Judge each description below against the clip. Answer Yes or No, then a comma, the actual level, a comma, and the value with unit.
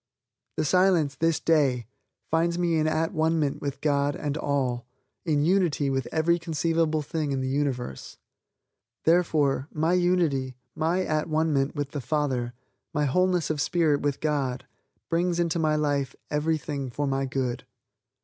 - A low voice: No, medium, 150 Hz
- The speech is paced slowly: No, average, 155 wpm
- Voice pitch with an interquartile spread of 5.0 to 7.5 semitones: No, average, 2.9 semitones